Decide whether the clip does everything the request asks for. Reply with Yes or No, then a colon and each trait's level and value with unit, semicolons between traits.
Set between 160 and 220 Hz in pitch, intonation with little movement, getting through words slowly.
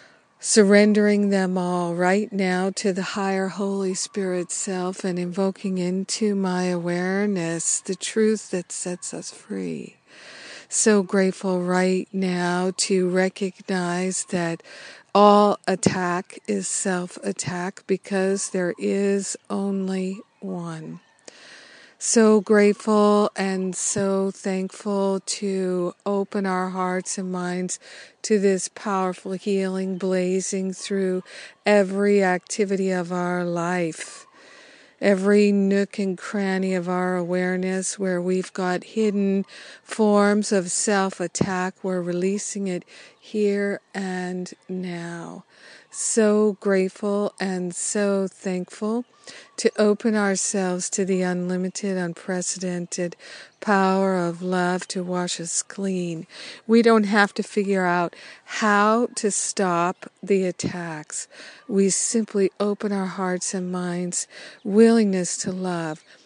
Yes: high, 190 Hz; narrow, 1.9 semitones; slow, 110 wpm